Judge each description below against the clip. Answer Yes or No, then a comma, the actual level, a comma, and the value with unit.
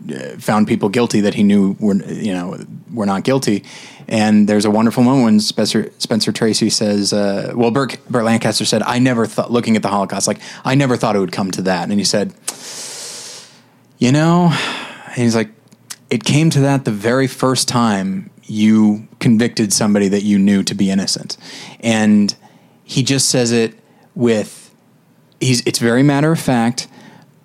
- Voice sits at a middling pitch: No, low, 115 Hz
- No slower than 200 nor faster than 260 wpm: No, average, 175 wpm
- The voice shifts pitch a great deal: No, average, 4.3 semitones